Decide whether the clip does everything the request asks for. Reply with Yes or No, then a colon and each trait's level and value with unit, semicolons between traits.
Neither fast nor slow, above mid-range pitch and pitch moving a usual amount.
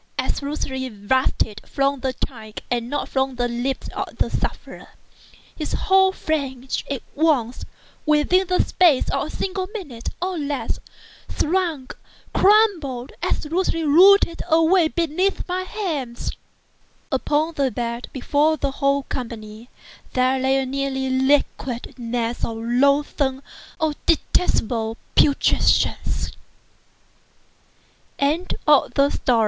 No: slow, 110 wpm; very high, 280 Hz; average, 4.2 semitones